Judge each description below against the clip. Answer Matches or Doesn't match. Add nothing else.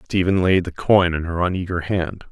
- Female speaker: Doesn't match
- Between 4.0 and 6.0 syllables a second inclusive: Matches